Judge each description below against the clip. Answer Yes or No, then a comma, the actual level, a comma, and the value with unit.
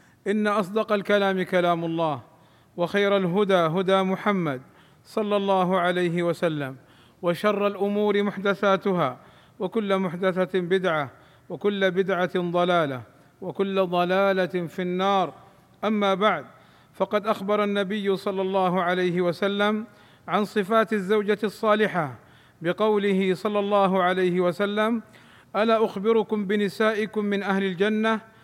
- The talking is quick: No, average, 105 wpm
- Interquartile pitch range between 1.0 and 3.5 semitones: Yes, average, 2.7 semitones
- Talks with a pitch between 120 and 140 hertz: No, high, 195 Hz